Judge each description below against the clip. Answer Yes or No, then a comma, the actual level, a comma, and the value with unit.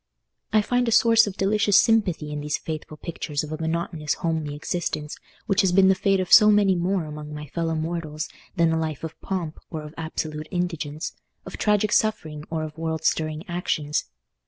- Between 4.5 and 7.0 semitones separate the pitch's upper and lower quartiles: No, average, 3.8 semitones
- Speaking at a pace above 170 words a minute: Yes, average, 190 wpm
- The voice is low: No, medium, 165 Hz